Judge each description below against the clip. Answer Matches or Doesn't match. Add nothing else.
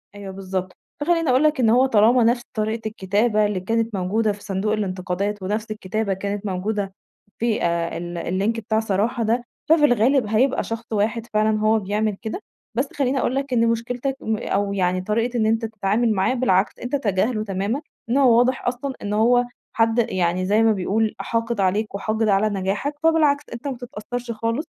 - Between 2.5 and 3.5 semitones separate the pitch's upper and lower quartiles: Matches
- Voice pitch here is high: Matches